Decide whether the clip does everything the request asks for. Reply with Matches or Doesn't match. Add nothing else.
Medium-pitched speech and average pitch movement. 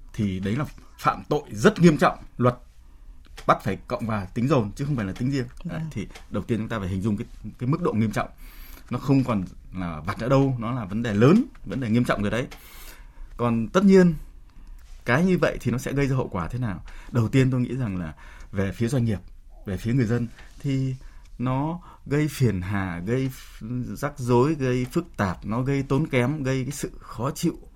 Doesn't match